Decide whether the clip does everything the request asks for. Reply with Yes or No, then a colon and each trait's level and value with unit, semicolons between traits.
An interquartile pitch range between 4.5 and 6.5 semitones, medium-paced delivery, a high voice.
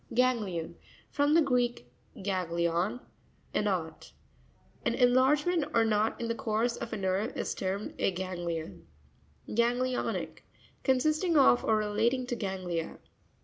No: average, 5.2 semitones; slow, 125 wpm; high, 225 Hz